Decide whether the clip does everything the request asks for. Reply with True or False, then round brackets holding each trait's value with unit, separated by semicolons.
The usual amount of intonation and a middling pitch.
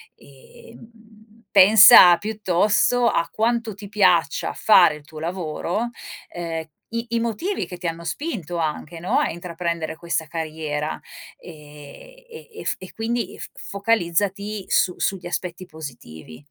True (5.0 semitones; 180 Hz)